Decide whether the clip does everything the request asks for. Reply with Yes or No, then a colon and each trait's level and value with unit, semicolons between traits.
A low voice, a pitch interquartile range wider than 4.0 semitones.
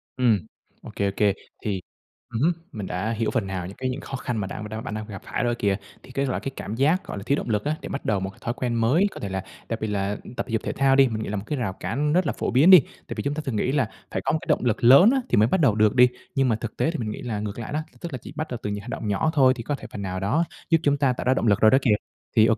Yes: low, 120 Hz; average, 4.7 semitones